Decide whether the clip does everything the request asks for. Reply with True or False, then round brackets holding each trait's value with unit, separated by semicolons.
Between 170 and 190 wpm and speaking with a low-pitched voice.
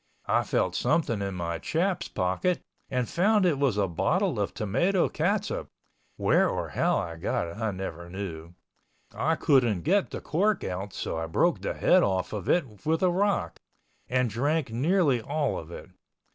True (175 wpm; 125 Hz)